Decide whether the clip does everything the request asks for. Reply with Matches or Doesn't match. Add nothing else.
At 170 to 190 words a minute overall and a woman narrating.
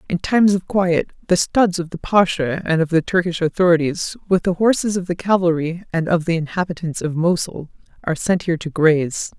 Doesn't match